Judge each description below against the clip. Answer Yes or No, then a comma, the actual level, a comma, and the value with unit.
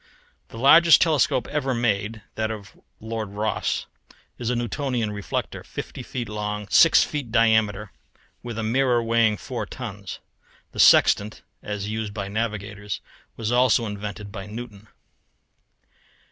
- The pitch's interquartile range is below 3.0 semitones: Yes, narrow, 2.6 semitones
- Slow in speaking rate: Yes, slow, 130 wpm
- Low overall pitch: Yes, low, 110 Hz